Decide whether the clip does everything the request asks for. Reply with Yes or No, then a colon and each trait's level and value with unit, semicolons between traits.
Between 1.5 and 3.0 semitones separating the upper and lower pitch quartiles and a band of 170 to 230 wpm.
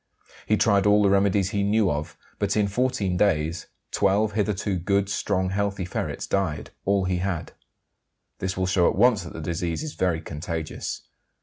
Yes: narrow, 2.5 semitones; average, 175 wpm